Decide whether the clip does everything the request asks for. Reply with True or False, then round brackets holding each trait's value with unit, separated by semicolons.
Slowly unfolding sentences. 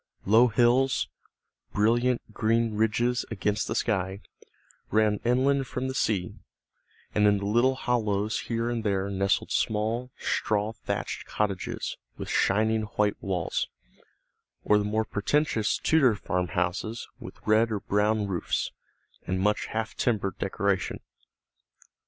True (125 wpm)